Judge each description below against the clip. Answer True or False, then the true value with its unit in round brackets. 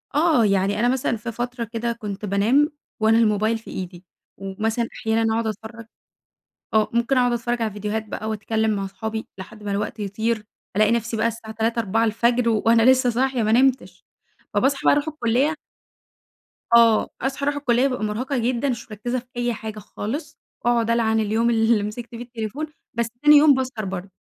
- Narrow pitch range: True (2.1 semitones)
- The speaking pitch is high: True (230 Hz)